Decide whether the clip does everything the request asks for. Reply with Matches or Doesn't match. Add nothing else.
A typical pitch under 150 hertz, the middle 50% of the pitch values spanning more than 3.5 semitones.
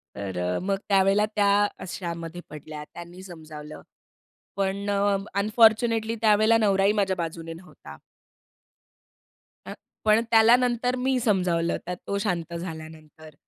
Doesn't match